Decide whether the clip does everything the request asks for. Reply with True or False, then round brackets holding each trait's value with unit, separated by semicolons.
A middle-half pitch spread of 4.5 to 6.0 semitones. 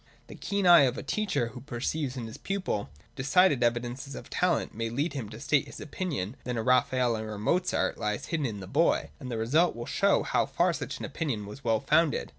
True (5.2 semitones)